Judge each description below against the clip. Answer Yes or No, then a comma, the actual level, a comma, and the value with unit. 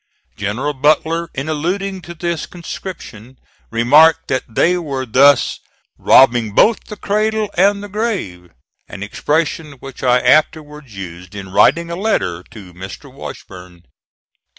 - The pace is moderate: No, slow, 130 wpm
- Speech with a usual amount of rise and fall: No, wide, 7.8 semitones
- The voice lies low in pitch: No, medium, 145 Hz